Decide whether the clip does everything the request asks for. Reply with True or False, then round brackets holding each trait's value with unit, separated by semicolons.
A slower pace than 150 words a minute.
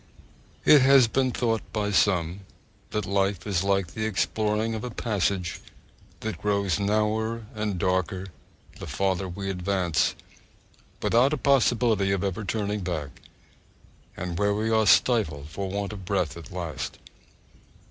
True (140 wpm)